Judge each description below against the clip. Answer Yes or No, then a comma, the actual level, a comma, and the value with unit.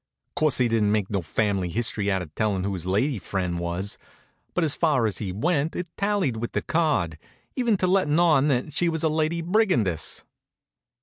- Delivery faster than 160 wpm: Yes, average, 195 wpm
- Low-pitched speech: Yes, low, 125 Hz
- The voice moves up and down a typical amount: No, wide, 8.7 semitones